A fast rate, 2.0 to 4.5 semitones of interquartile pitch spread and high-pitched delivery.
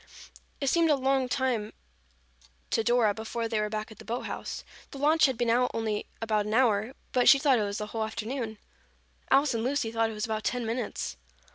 Yes: fast, 215 wpm; average, 3.2 semitones; high, 230 Hz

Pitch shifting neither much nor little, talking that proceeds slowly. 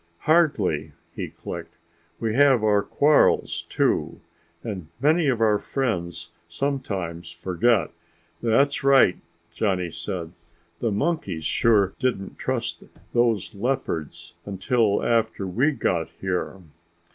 No: wide, 6.5 semitones; slow, 110 wpm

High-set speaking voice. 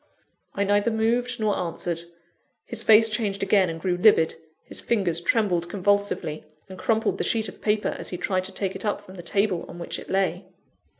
Yes: high, 195 Hz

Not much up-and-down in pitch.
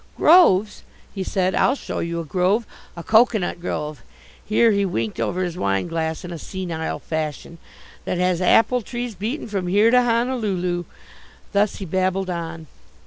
No: average, 4.3 semitones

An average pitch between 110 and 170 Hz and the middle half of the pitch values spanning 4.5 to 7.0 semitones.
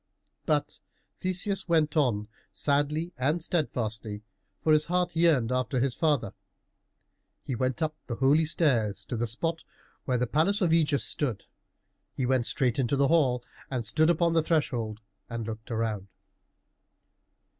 Yes: medium, 140 Hz; average, 5.3 semitones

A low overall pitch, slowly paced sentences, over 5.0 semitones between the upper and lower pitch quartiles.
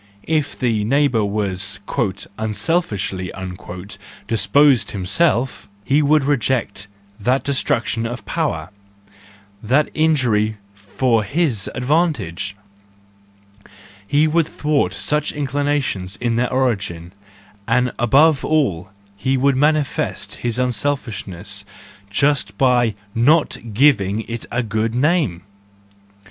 Yes: low, 120 Hz; slow, 100 wpm; wide, 5.6 semitones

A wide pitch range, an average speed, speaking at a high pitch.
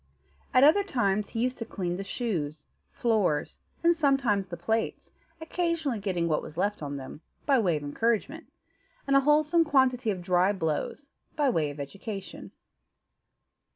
Yes: wide, 7.7 semitones; average, 155 wpm; high, 215 Hz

